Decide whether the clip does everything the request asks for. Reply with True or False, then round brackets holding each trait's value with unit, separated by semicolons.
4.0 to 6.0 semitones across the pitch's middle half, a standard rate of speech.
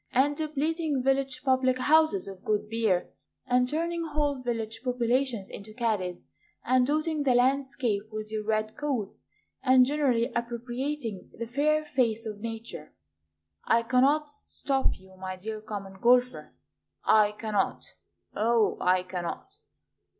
False (4.4 semitones; 130 wpm)